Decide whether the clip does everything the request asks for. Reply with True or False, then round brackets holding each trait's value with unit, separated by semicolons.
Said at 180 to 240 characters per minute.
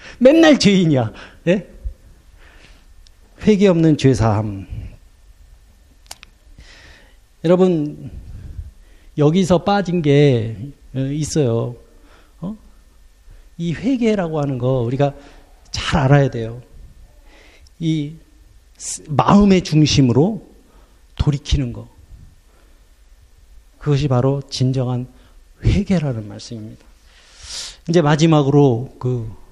False (165 characters per minute)